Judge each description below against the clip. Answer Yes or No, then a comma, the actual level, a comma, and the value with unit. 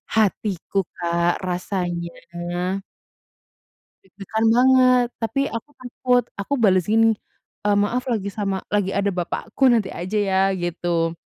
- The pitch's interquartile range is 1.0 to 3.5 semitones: No, average, 3.9 semitones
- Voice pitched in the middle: No, high, 200 Hz